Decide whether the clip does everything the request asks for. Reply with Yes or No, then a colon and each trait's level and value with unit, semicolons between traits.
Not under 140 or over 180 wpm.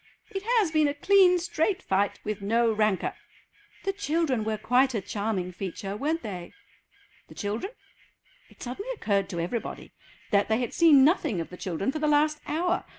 Yes: average, 175 wpm